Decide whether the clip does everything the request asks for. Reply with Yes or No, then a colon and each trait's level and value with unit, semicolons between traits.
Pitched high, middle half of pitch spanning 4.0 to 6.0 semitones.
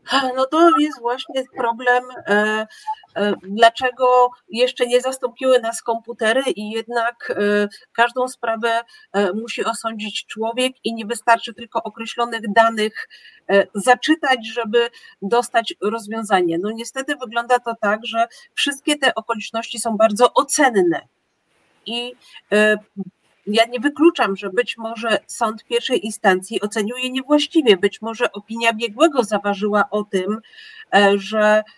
No: high, 230 Hz; average, 3.0 semitones